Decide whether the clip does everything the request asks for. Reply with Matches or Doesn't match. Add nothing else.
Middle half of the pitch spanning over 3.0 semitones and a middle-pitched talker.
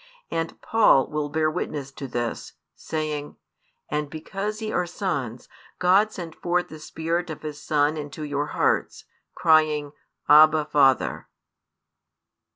Doesn't match